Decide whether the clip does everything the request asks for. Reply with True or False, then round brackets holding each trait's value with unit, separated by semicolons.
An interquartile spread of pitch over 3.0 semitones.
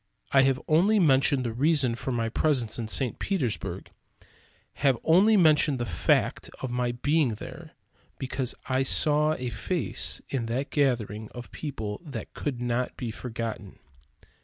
True (4.0 semitones)